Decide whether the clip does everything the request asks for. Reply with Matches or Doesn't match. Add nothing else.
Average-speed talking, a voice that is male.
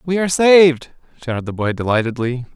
Matches